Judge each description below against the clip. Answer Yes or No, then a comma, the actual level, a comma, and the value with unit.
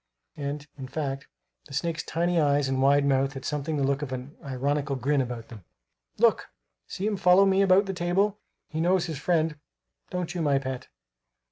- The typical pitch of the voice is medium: Yes, medium, 145 Hz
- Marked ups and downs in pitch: No, average, 4.3 semitones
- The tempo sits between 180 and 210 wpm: Yes, average, 190 wpm